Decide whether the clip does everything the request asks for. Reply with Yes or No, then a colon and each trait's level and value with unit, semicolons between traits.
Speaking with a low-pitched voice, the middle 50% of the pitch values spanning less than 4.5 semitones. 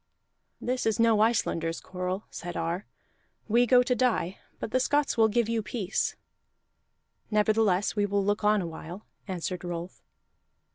No: high, 210 Hz; average, 4.0 semitones